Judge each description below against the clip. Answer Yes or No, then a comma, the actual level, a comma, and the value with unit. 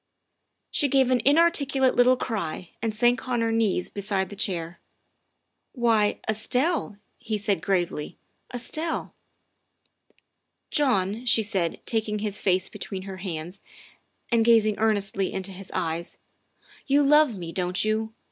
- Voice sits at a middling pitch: No, high, 215 Hz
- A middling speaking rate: Yes, average, 150 wpm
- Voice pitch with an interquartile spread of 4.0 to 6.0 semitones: Yes, average, 4.4 semitones